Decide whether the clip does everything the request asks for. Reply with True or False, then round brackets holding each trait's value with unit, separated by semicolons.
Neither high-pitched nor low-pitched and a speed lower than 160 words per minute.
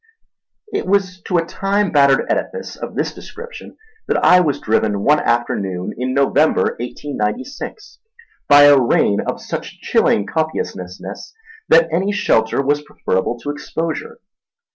True (145 Hz; 135 wpm)